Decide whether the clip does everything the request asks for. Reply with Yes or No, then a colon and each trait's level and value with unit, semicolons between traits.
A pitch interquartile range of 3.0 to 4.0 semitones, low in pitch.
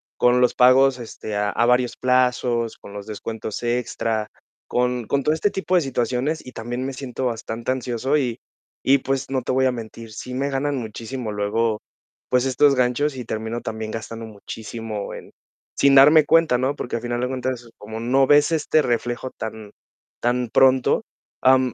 No: narrow, 2.6 semitones; low, 125 Hz